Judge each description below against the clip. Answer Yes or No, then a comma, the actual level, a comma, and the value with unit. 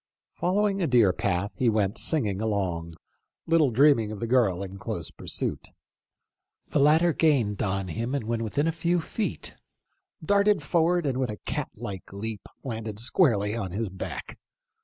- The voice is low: Yes, low, 115 Hz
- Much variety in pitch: Yes, wide, 7.4 semitones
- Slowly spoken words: No, average, 160 wpm